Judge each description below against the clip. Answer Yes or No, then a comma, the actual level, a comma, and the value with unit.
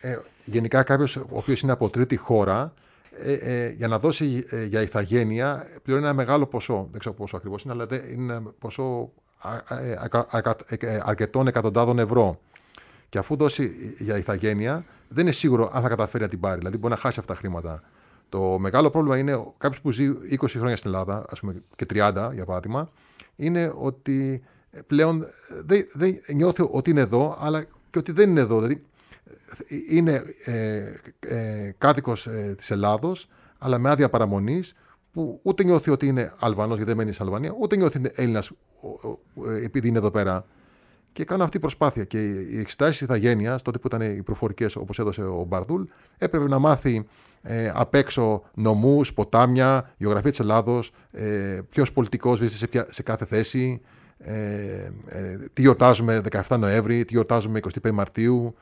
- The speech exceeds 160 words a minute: Yes, fast, 170 wpm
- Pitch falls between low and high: No, low, 120 Hz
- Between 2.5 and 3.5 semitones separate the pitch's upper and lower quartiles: No, average, 4.3 semitones